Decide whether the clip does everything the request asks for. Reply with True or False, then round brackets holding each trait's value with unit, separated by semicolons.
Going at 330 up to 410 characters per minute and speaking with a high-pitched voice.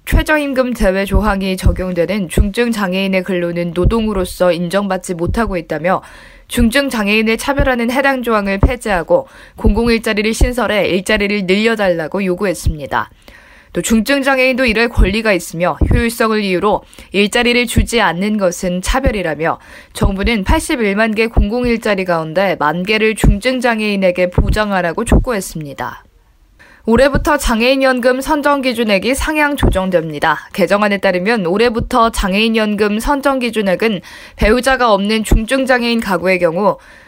True (340 characters per minute; 215 Hz)